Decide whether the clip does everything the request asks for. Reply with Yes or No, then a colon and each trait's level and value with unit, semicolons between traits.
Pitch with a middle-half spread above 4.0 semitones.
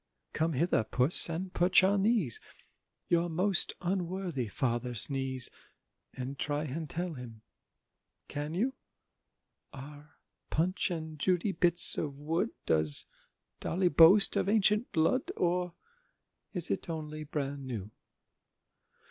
Yes: average, 4.7 semitones